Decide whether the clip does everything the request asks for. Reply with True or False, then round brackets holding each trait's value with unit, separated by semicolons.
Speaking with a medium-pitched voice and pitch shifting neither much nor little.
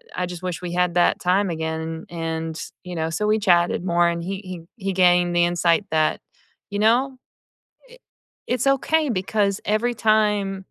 True (180 Hz; 3.5 semitones)